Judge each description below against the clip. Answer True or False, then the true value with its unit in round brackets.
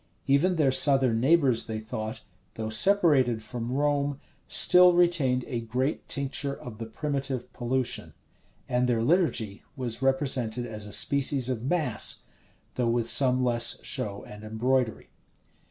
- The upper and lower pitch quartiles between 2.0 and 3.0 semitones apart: False (3.5 semitones)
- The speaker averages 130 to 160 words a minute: True (140 wpm)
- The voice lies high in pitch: False (125 Hz)